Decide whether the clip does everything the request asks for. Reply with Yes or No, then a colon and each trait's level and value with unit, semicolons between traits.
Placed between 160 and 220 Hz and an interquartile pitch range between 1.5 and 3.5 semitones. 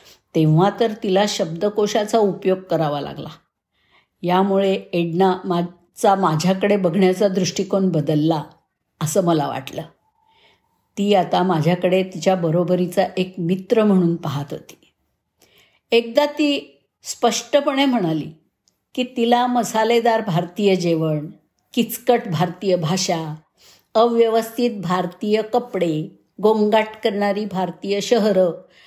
No: high, 190 Hz; average, 4.0 semitones